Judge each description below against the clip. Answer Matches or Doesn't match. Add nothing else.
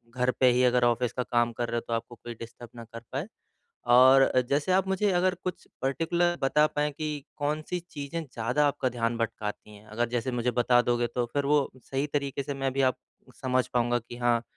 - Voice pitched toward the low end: Matches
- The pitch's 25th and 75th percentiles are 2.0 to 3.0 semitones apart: Doesn't match